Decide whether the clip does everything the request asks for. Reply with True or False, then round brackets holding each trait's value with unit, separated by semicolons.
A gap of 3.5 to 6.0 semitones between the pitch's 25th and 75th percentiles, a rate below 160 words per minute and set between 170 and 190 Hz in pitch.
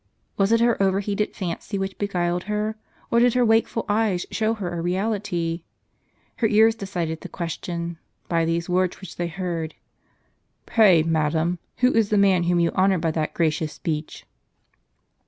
False (3.8 semitones; 170 wpm; 185 Hz)